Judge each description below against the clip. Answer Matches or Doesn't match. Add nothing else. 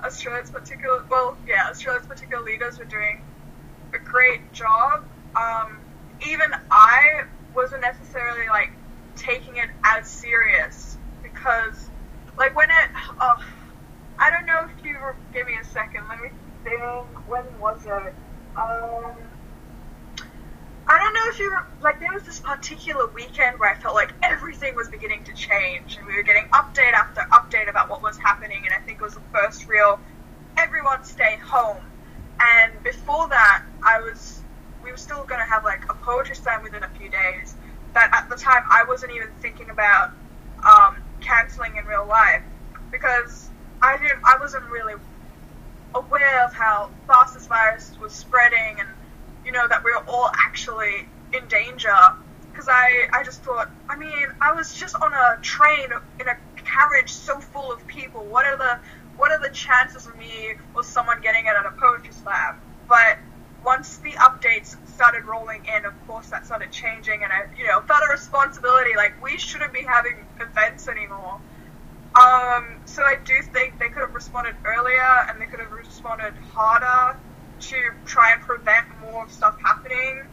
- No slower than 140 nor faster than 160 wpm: Doesn't match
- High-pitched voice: Matches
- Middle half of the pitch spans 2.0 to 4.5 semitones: Matches